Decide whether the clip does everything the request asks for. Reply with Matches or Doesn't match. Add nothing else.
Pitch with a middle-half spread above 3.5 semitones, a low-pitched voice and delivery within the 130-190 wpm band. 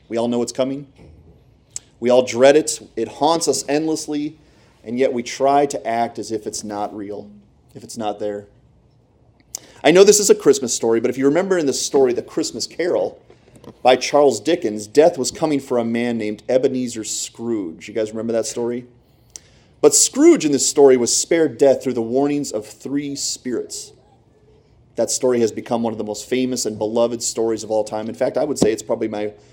Doesn't match